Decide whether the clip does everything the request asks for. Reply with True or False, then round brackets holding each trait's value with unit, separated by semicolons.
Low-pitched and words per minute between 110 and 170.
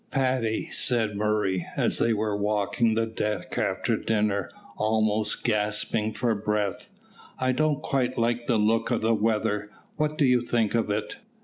True (110 Hz; 155 wpm)